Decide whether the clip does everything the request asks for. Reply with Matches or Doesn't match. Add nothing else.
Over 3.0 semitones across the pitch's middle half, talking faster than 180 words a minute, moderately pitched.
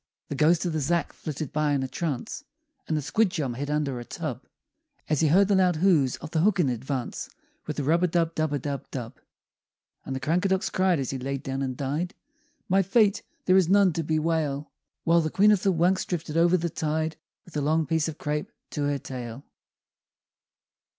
Matches